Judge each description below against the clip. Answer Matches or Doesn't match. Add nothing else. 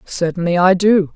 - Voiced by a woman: Matches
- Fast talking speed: Doesn't match